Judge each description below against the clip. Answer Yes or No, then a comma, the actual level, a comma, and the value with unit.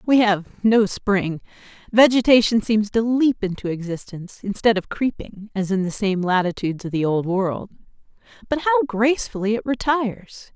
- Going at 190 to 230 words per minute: No, average, 155 wpm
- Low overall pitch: No, high, 215 Hz